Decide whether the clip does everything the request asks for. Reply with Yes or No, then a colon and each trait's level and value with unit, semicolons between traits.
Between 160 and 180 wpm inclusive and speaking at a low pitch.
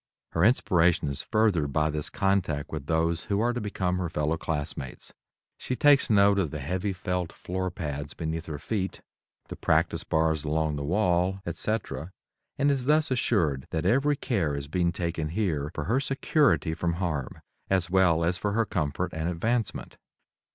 Yes: average, 170 wpm; very low, 90 Hz